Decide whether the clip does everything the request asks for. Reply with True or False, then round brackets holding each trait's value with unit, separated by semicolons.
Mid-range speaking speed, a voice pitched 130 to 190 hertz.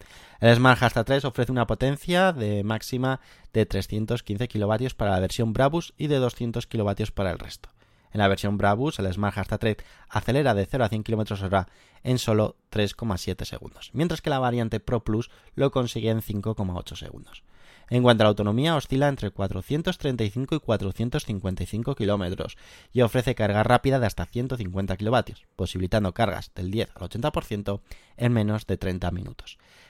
False (165 wpm; 110 Hz)